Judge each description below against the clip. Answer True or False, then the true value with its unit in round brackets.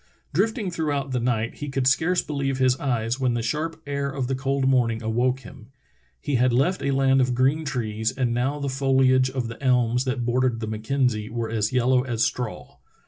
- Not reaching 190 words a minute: False (200 wpm)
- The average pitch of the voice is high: False (130 Hz)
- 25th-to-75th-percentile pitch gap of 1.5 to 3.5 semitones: True (2.5 semitones)